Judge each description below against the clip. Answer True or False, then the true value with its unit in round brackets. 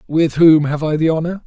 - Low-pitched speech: False (160 Hz)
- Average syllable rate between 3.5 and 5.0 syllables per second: False (5.4 syllables/s)